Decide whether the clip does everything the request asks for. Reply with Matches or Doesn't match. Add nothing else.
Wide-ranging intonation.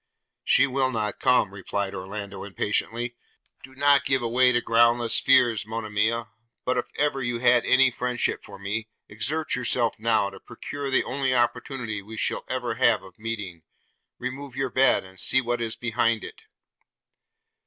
Doesn't match